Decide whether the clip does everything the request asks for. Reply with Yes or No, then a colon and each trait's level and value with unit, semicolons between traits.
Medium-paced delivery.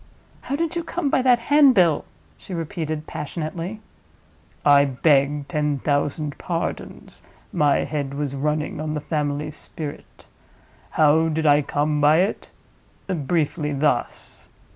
No: slow, 120 wpm